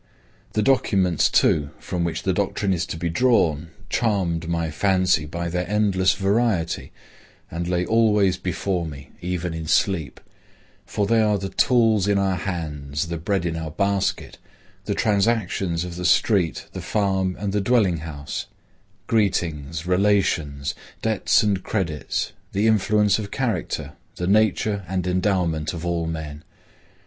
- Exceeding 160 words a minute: No, average, 145 wpm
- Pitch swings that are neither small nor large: Yes, average, 3.7 semitones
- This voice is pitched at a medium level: No, very low, 90 Hz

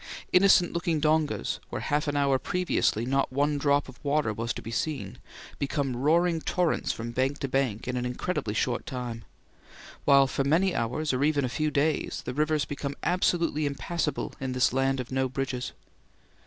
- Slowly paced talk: No, average, 180 wpm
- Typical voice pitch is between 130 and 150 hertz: Yes, medium, 140 Hz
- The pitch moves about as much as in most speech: Yes, average, 3.2 semitones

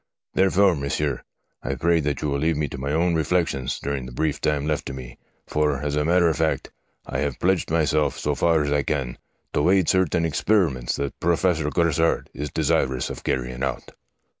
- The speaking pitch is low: Yes, very low, 75 Hz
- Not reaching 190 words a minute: No, average, 195 wpm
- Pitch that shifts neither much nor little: Yes, average, 3.0 semitones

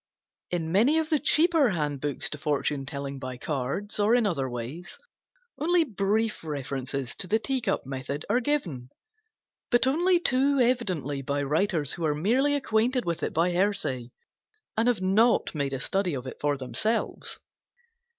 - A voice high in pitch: No, medium, 180 Hz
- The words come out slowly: No, average, 160 wpm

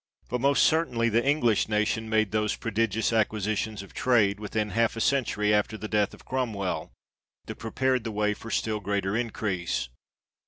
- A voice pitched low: Yes, low, 110 Hz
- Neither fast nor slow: Yes, average, 165 wpm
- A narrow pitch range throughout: Yes, narrow, 1.9 semitones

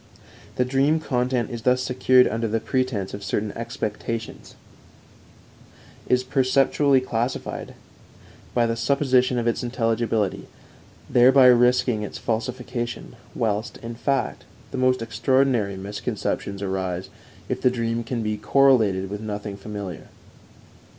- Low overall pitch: Yes, low, 120 Hz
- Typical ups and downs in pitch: Yes, average, 3.2 semitones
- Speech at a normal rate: No, slow, 120 wpm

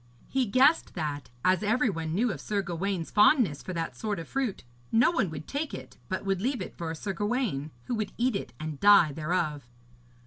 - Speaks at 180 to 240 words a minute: Yes, fast, 205 wpm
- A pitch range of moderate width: No, wide, 6.4 semitones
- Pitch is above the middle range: Yes, high, 195 Hz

